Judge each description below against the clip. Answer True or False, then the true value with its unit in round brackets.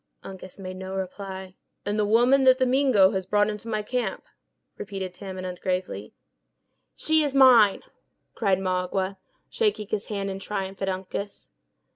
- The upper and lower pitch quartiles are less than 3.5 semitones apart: True (2.5 semitones)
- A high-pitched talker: True (195 Hz)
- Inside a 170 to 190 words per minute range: False (150 wpm)